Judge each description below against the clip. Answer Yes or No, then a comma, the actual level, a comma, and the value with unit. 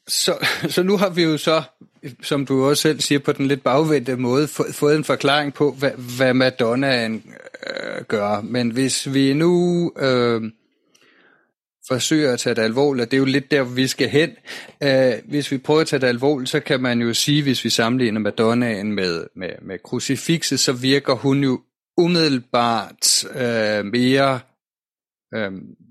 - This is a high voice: No, low, 135 Hz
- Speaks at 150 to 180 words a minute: Yes, average, 175 wpm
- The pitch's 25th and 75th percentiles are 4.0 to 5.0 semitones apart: No, average, 3.2 semitones